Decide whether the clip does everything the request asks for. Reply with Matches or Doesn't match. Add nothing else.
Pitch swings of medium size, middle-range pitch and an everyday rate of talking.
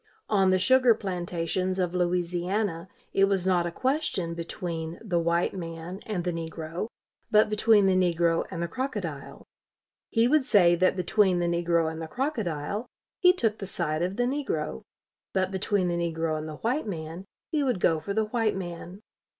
Matches